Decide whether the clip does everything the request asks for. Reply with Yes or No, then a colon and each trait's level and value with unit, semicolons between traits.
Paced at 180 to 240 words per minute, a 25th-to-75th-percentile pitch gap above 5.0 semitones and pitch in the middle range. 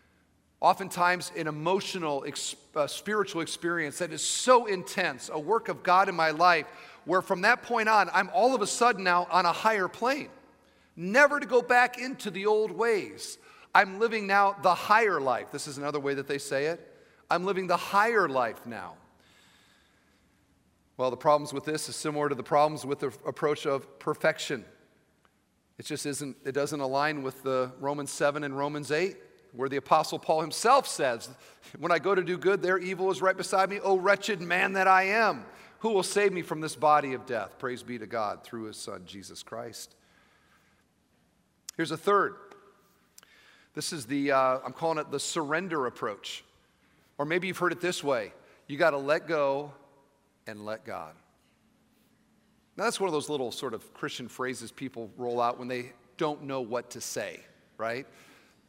Yes: average, 185 wpm; wide, 5.5 semitones; medium, 155 Hz